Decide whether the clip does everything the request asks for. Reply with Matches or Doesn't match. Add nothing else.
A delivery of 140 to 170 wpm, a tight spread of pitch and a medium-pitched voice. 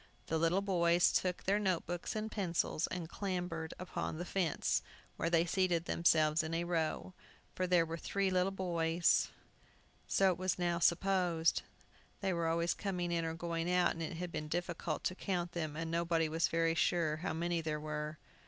Doesn't match